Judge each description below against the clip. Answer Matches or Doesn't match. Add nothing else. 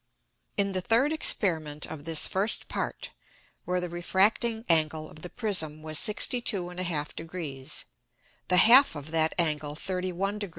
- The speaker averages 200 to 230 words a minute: Doesn't match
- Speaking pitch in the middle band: Matches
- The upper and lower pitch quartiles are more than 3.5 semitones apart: Matches